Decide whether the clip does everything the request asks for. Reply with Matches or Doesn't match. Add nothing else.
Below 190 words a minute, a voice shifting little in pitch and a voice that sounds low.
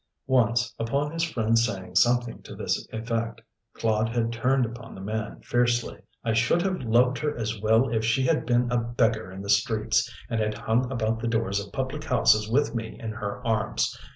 Doesn't match